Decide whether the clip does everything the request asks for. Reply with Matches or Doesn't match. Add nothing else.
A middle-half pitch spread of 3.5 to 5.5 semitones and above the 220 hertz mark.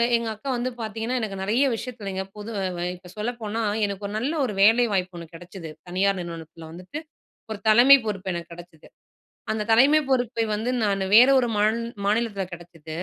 Doesn't match